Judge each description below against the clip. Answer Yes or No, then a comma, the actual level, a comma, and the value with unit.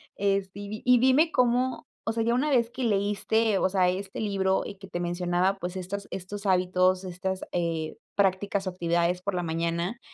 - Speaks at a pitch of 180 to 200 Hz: Yes, high, 190 Hz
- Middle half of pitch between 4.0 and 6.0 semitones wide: No, average, 2.7 semitones